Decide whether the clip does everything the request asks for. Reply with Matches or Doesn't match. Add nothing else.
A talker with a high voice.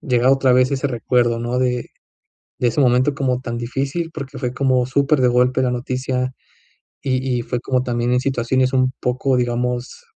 Doesn't match